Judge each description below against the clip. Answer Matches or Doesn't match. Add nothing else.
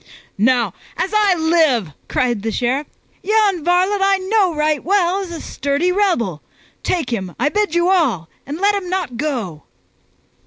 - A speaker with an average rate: Matches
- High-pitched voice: Matches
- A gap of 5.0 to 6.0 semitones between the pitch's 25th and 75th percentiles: Doesn't match